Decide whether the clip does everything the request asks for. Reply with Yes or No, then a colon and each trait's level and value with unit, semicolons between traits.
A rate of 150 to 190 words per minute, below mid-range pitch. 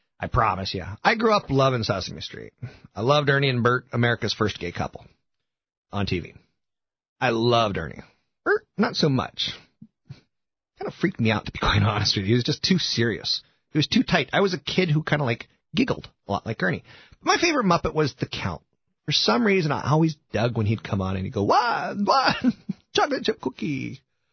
No: fast, 205 wpm; low, 130 Hz